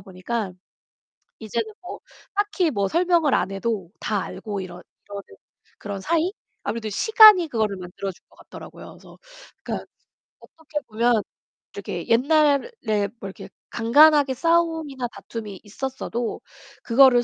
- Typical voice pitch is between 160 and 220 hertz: No, high, 235 Hz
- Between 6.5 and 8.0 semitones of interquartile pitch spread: Yes, wide, 7.2 semitones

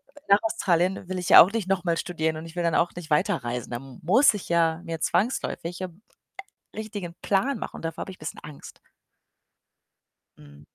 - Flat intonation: No, average, 3.2 semitones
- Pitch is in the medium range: Yes, medium, 175 Hz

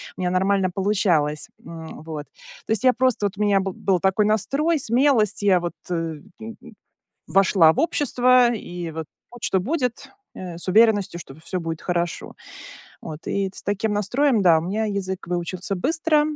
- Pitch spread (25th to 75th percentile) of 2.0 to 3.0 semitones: No, average, 4.4 semitones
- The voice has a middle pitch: No, high, 195 Hz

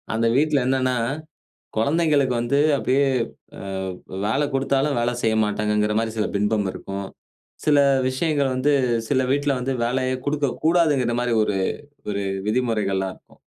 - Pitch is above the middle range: No, low, 130 Hz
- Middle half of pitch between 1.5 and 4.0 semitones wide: No, average, 4.5 semitones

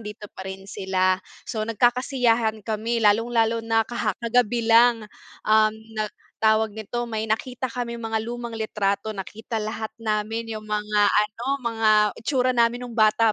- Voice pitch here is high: Yes, high, 225 Hz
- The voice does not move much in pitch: Yes, narrow, 1.7 semitones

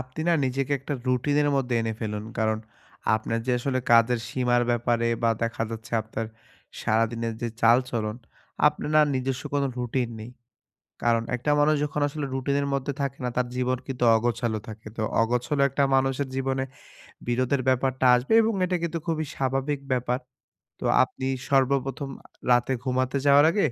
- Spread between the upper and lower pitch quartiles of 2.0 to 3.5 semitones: Yes, average, 2.7 semitones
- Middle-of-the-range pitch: No, low, 130 Hz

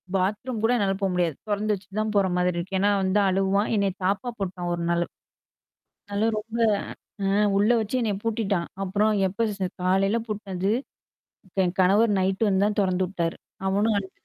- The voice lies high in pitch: Yes, high, 195 Hz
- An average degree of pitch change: No, narrow, 2.2 semitones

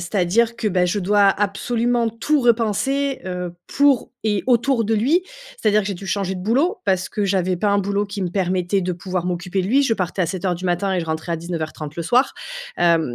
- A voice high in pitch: Yes, high, 195 Hz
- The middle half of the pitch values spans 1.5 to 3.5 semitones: No, average, 4.2 semitones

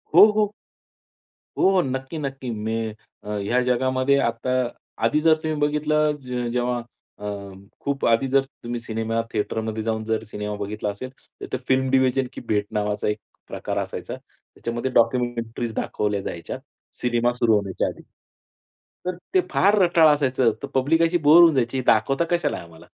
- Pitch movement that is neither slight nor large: Yes, average, 3.8 semitones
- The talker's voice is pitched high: No, low, 125 Hz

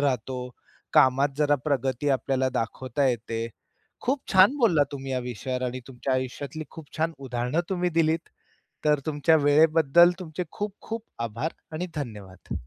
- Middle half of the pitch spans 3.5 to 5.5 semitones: Yes, average, 4.1 semitones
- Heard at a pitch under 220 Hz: Yes, medium, 140 Hz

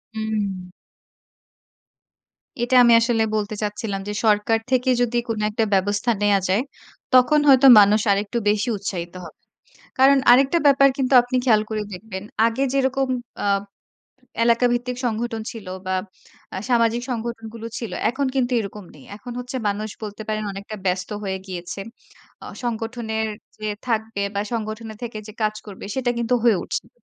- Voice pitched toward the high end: Yes, high, 225 Hz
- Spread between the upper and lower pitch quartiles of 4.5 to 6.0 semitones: No, average, 2.8 semitones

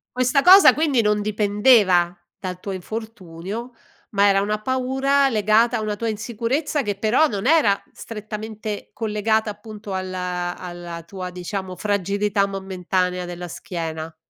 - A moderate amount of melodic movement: Yes, average, 3.6 semitones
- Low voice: No, high, 205 Hz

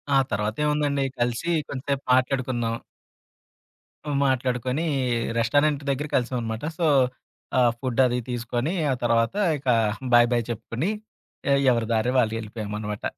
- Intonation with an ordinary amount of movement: Yes, average, 3.1 semitones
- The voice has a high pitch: No, low, 125 Hz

